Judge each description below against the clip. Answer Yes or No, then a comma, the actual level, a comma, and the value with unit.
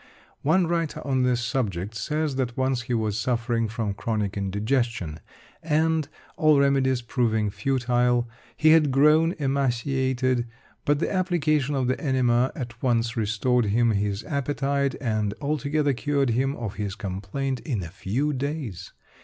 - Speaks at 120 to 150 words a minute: Yes, average, 145 wpm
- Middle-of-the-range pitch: No, low, 130 Hz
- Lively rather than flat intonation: No, average, 3.9 semitones